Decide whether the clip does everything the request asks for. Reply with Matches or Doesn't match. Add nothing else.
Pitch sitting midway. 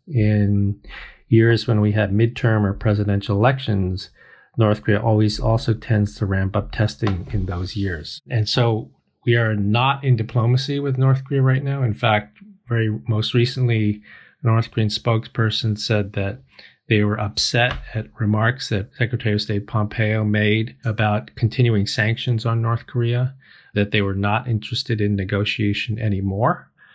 Doesn't match